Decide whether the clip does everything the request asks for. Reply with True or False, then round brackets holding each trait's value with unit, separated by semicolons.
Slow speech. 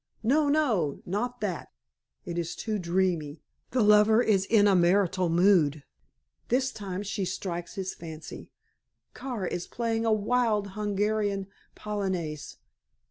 True (130 wpm)